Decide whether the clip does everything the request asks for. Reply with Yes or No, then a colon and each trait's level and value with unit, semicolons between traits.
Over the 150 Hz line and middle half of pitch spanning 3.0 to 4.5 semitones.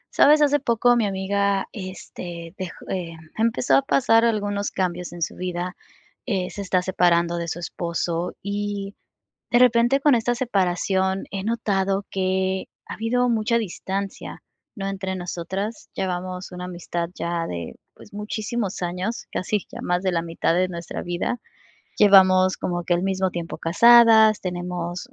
Yes: high, 190 Hz; average, 3.4 semitones